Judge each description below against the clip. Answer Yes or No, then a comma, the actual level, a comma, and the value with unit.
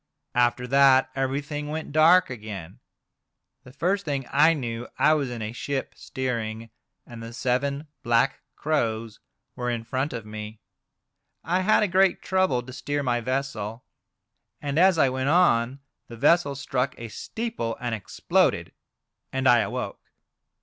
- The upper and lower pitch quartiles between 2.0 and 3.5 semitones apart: No, average, 4.0 semitones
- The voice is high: No, low, 130 Hz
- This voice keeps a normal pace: Yes, average, 150 wpm